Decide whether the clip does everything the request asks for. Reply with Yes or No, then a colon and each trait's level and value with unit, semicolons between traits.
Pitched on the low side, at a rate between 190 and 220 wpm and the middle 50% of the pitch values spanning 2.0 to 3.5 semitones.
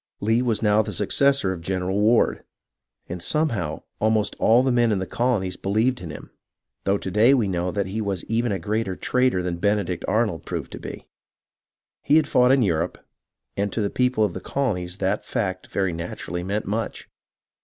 No: low, 105 Hz; average, 195 wpm; average, 4.1 semitones